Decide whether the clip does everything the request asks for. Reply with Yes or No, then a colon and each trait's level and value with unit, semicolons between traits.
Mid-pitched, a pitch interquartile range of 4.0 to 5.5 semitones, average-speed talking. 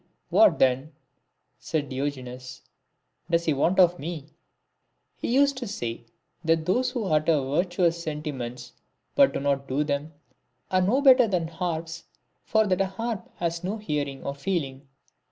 Yes: medium, 165 Hz; average, 5.2 semitones; average, 165 wpm